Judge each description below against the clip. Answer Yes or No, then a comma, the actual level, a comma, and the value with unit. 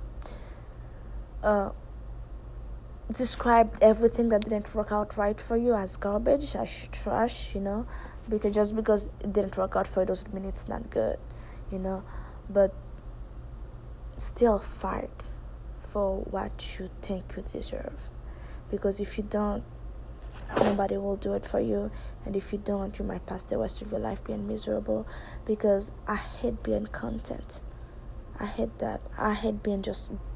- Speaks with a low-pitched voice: No, high, 195 Hz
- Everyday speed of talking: Yes, average, 150 wpm